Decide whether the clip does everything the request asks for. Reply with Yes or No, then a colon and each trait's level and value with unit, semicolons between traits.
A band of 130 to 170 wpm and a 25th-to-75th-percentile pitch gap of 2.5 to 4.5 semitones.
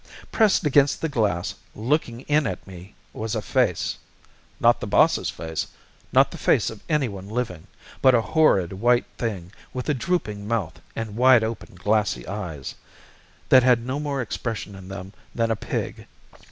No: average, 165 wpm; average, 4.9 semitones